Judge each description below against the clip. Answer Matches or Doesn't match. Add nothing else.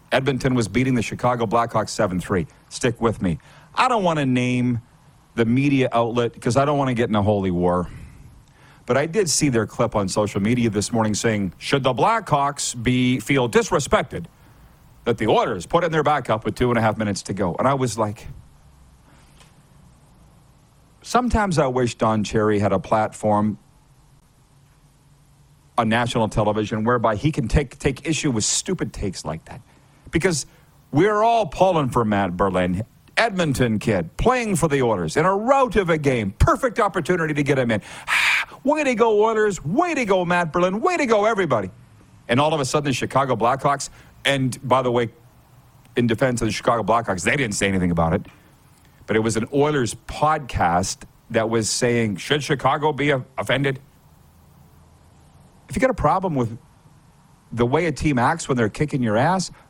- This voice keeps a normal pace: Matches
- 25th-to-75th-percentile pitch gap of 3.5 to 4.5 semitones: Doesn't match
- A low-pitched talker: Matches